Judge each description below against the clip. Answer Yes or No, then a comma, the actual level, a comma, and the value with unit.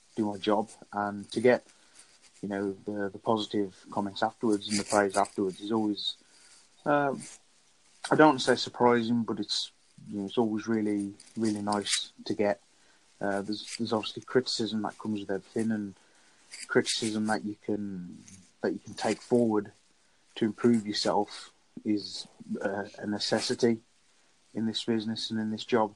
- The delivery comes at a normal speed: Yes, average, 160 wpm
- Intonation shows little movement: Yes, narrow, 1.7 semitones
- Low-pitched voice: Yes, low, 105 Hz